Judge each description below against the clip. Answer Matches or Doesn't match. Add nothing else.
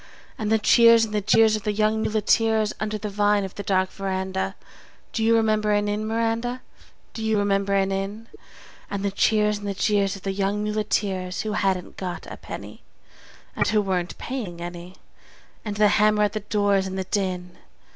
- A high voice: Matches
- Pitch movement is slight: Matches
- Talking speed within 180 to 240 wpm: Matches